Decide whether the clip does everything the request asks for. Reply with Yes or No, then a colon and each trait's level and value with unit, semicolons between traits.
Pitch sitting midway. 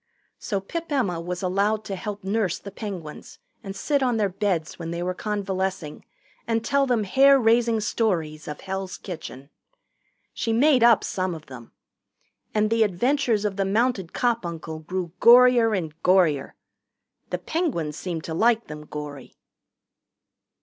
No: high, 195 Hz